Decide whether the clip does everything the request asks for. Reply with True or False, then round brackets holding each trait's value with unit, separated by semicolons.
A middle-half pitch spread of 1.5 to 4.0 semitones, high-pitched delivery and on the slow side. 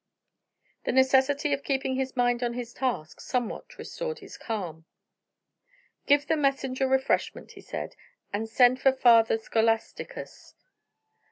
True (2.8 semitones; 255 Hz; 125 wpm)